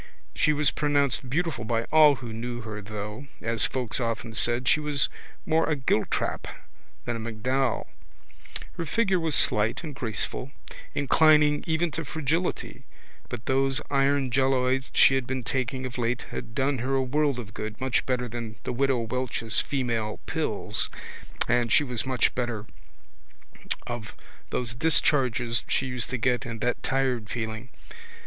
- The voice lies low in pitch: Yes, low, 125 Hz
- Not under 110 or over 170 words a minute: Yes, average, 155 wpm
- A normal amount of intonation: Yes, average, 3.0 semitones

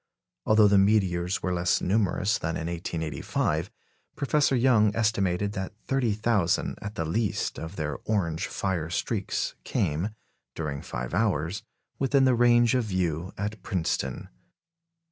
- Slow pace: Yes, slow, 130 wpm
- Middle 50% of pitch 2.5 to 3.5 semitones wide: No, average, 4.5 semitones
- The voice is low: Yes, very low, 95 Hz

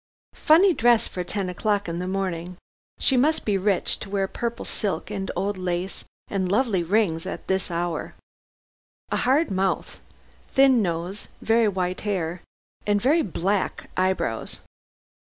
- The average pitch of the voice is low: No, high, 195 Hz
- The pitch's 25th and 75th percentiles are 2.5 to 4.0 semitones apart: Yes, average, 3.3 semitones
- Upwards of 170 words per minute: No, average, 145 wpm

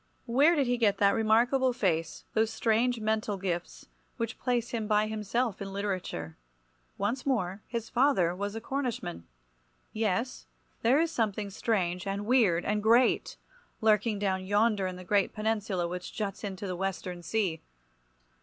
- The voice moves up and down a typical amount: Yes, average, 3.4 semitones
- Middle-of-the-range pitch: No, high, 210 Hz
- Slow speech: No, average, 155 wpm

